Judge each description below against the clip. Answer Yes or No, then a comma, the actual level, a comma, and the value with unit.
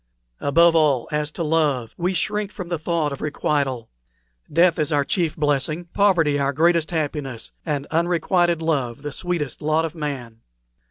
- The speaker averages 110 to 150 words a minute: No, average, 160 wpm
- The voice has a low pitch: No, medium, 155 Hz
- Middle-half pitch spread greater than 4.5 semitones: No, average, 3.0 semitones